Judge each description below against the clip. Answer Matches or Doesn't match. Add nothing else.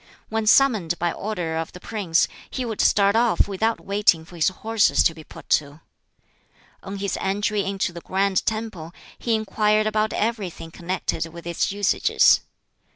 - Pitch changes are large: Doesn't match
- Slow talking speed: Doesn't match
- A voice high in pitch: Matches